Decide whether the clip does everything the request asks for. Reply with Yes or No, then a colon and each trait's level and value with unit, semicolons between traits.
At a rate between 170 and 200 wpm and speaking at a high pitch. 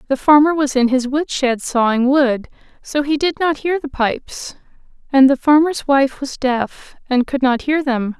Yes: average, 190 wpm; very high, 275 Hz